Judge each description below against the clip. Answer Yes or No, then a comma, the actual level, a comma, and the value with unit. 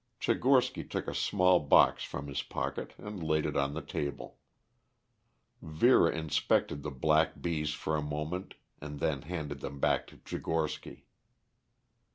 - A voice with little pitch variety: Yes, narrow, 2.0 semitones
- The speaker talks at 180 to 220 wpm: No, average, 145 wpm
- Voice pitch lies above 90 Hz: No, very low, 75 Hz